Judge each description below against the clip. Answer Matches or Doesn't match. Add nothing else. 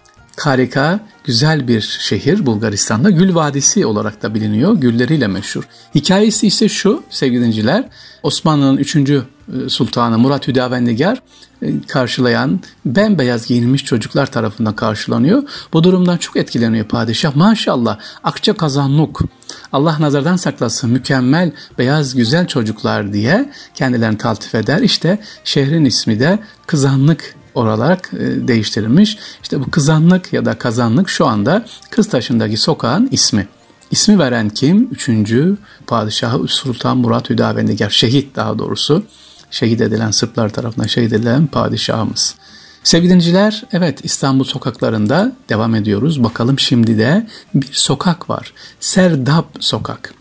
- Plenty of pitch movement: Matches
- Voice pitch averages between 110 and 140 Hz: Matches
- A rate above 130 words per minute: Doesn't match